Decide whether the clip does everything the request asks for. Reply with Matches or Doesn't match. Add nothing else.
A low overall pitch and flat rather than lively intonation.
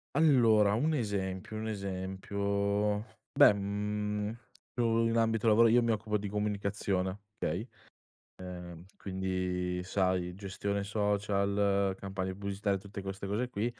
Matches